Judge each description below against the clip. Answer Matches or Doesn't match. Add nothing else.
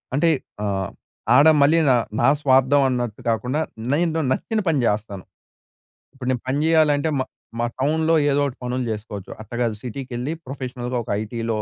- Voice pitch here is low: Matches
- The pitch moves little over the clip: Doesn't match